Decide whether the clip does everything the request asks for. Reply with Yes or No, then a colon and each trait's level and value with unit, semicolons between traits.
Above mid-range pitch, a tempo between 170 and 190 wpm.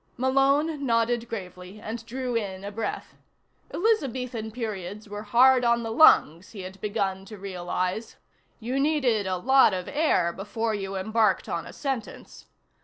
No: high, 220 Hz; average, 150 wpm